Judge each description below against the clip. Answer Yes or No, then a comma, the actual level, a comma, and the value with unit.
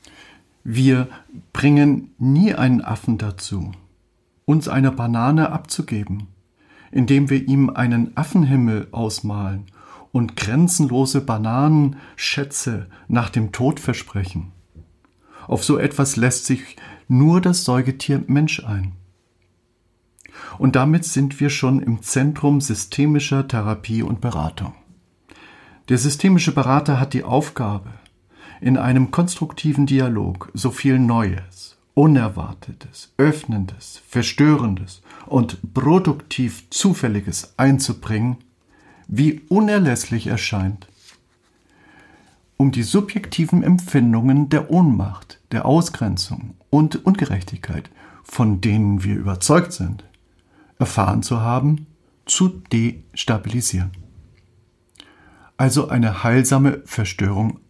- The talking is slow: Yes, slow, 95 wpm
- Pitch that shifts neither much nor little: No, wide, 5.7 semitones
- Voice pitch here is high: No, low, 125 Hz